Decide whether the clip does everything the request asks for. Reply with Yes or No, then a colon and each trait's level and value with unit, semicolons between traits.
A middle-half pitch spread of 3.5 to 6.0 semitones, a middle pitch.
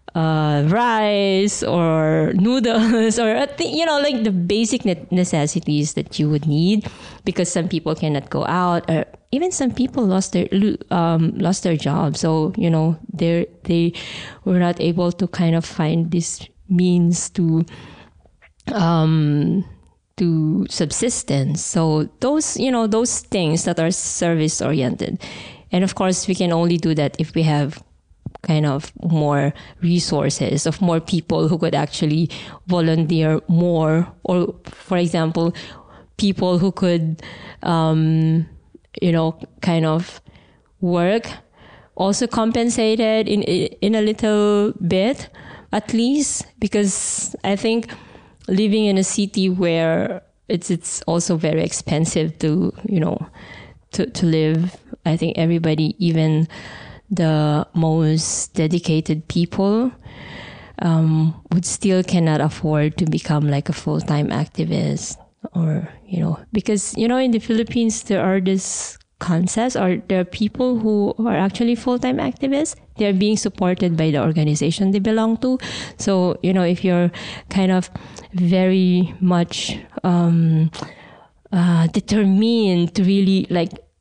Yes: average, 4.2 semitones; medium, 175 Hz